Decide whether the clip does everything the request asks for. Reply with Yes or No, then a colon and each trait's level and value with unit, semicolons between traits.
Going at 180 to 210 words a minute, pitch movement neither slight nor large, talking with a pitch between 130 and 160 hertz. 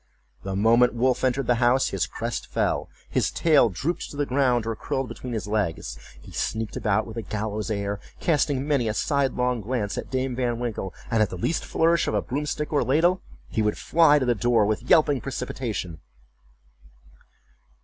No: average, 190 wpm; average, 4.2 semitones; low, 120 Hz